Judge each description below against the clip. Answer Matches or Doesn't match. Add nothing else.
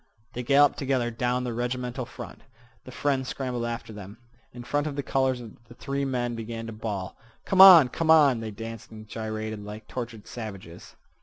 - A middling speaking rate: Matches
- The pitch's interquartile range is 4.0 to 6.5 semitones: Doesn't match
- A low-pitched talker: Matches